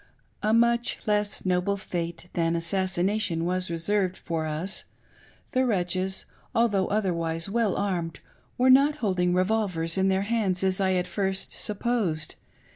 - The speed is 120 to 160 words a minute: Yes, average, 140 wpm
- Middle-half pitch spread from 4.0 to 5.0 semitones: No, average, 3.0 semitones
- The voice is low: No, high, 190 Hz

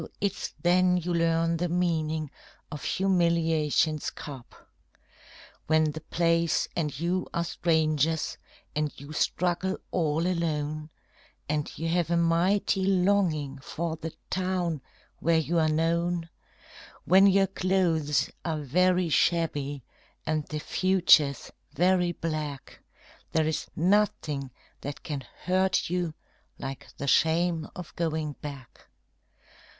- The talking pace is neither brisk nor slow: No, slow, 115 wpm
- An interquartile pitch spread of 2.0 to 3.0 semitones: Yes, narrow, 2.6 semitones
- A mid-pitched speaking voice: Yes, medium, 165 Hz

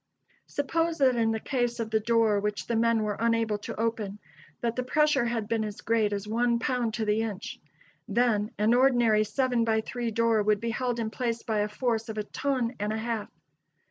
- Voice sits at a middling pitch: No, high, 230 Hz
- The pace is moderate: No, fast, 210 wpm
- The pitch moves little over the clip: Yes, narrow, 2.1 semitones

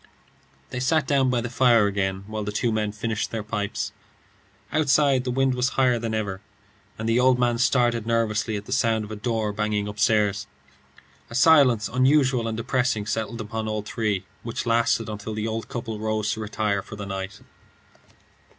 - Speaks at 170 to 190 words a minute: Yes, average, 180 wpm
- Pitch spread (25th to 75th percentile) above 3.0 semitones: No, average, 2.7 semitones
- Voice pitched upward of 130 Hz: No, low, 110 Hz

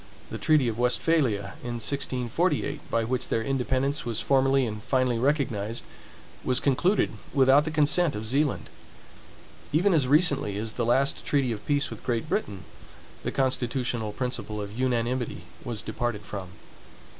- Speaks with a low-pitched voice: Yes, low, 130 Hz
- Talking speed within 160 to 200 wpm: No, average, 145 wpm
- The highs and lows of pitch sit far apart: No, average, 3.6 semitones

